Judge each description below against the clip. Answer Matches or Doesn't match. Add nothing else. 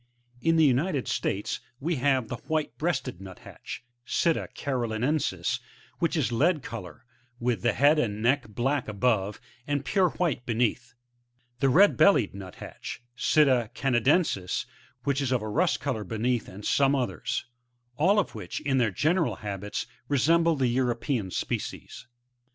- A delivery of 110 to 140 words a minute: Doesn't match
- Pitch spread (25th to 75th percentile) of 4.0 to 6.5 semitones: Matches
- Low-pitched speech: Matches